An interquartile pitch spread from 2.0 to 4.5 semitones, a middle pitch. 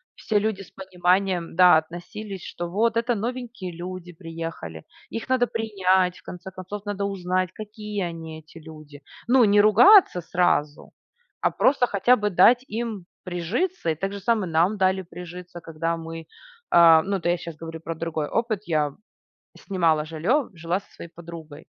Yes: average, 4.0 semitones; medium, 180 Hz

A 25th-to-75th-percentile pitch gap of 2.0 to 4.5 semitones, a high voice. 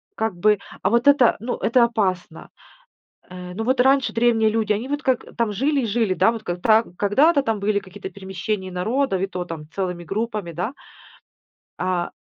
Yes: average, 4.2 semitones; high, 215 Hz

